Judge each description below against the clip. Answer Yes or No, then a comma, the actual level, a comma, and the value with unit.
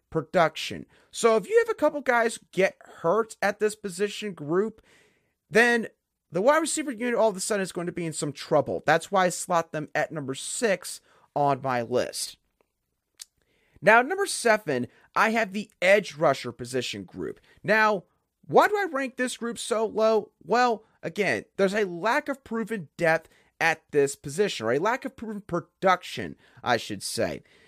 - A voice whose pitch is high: Yes, high, 200 Hz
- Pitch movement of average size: No, wide, 6.0 semitones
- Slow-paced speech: No, average, 175 wpm